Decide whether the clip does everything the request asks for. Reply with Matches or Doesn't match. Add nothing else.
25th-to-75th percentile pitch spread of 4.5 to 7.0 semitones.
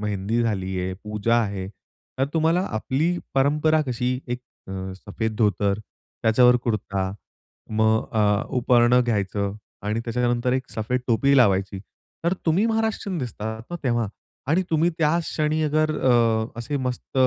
Matches